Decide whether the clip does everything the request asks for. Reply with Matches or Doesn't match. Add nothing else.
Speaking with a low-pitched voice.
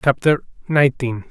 Matches